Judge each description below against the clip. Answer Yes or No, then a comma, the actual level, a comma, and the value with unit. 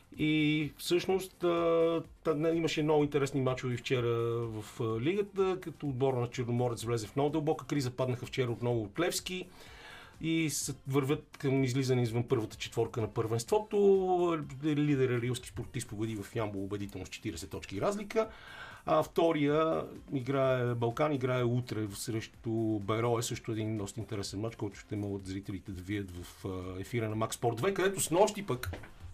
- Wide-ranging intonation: Yes, wide, 5.7 semitones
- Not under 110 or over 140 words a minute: No, average, 150 wpm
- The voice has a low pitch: Yes, low, 125 Hz